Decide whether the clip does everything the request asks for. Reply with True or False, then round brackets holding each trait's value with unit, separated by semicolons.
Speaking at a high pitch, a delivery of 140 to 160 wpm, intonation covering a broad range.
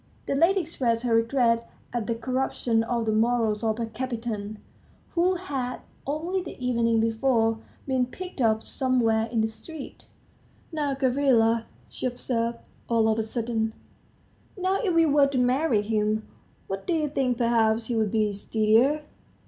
False (235 Hz; 155 wpm; 3.4 semitones)